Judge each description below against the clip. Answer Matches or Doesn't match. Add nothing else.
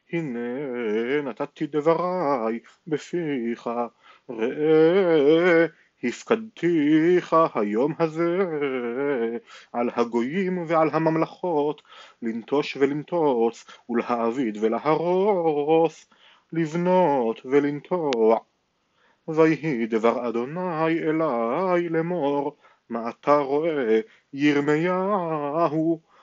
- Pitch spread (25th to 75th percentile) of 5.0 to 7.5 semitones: Matches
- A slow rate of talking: Matches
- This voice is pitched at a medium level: Matches